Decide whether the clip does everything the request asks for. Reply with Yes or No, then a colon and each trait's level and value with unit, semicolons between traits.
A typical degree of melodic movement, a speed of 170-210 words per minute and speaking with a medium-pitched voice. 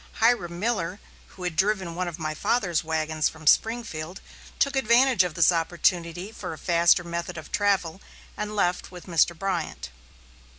No: average, 3.8 semitones; average, 160 wpm; medium, 175 Hz